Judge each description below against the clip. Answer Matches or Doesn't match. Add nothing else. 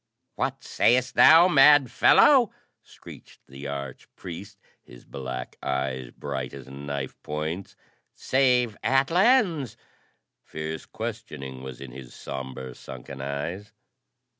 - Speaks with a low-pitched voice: Matches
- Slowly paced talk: Matches